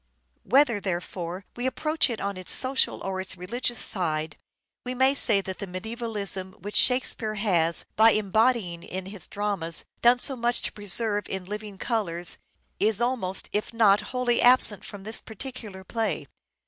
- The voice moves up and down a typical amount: Yes, average, 4.0 semitones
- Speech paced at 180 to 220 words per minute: No, average, 165 wpm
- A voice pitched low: No, high, 210 Hz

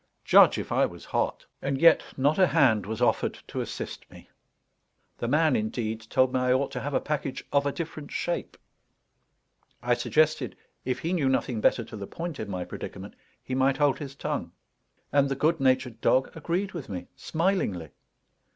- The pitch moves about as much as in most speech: Yes, average, 4.1 semitones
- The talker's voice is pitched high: No, low, 135 Hz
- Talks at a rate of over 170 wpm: Yes, average, 185 wpm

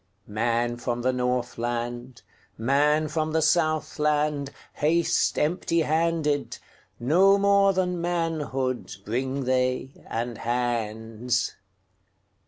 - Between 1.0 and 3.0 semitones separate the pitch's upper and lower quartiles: No, average, 4.7 semitones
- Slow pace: Yes, slow, 70 wpm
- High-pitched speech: No, low, 135 Hz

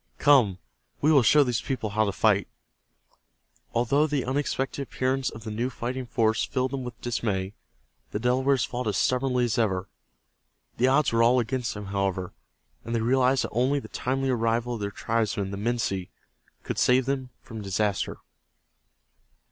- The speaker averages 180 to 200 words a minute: No, average, 165 wpm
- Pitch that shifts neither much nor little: Yes, average, 3.3 semitones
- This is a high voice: No, low, 120 Hz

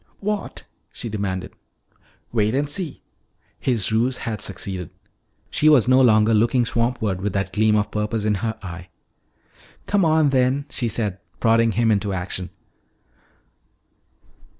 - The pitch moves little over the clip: No, average, 3.8 semitones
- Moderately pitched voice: No, low, 110 Hz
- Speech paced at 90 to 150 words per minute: Yes, slow, 135 wpm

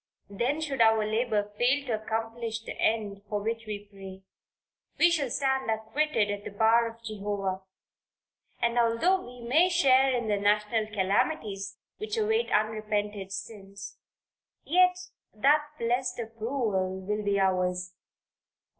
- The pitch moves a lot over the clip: No, average, 3.9 semitones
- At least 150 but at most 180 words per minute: No, slow, 135 wpm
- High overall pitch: Yes, high, 220 Hz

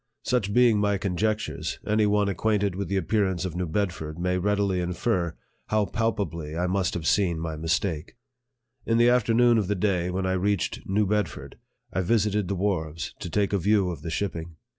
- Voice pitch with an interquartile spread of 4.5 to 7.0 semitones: No, average, 3.2 semitones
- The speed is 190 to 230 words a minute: Yes, average, 195 wpm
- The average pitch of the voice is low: Yes, very low, 95 Hz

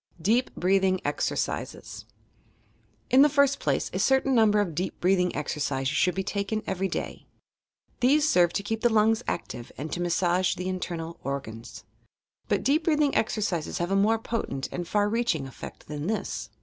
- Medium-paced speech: Yes, average, 165 wpm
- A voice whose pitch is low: No, high, 190 Hz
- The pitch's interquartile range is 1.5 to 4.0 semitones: No, average, 4.7 semitones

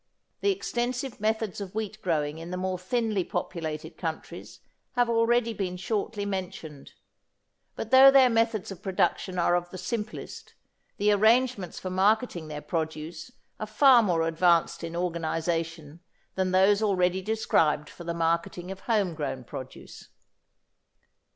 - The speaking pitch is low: No, medium, 185 Hz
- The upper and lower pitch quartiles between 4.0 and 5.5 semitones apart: Yes, average, 4.7 semitones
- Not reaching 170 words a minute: Yes, average, 140 wpm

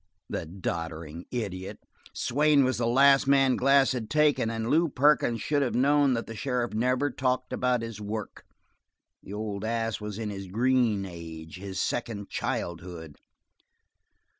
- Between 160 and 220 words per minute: No, average, 150 wpm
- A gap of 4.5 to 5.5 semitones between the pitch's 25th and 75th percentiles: Yes, average, 5.0 semitones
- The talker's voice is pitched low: Yes, low, 115 Hz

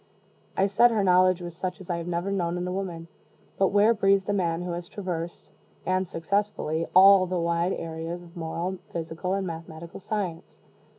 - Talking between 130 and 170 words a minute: No, average, 180 wpm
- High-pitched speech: No, medium, 180 Hz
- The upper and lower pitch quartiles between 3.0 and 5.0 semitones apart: No, narrow, 2.4 semitones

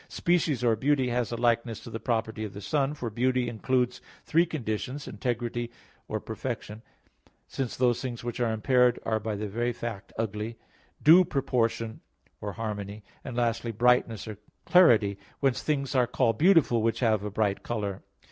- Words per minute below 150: No, average, 165 wpm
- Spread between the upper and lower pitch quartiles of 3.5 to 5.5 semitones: No, narrow, 2.6 semitones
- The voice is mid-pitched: No, low, 120 Hz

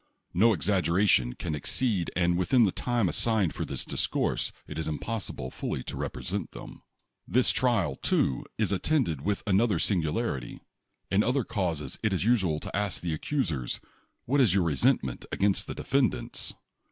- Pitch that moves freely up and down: Yes, wide, 6.0 semitones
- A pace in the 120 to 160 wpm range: No, average, 175 wpm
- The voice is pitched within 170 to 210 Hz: No, very low, 95 Hz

